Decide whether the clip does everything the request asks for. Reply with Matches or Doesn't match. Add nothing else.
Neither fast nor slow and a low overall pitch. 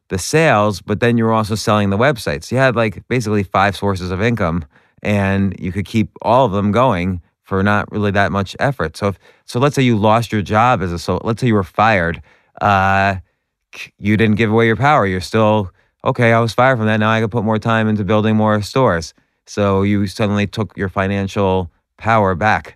Doesn't match